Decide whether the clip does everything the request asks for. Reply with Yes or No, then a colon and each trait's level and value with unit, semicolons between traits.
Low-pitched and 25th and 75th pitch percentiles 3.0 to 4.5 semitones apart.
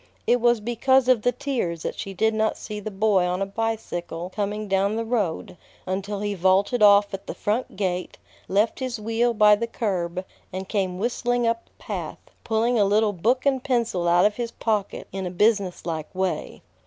No: high, 210 Hz; average, 3.4 semitones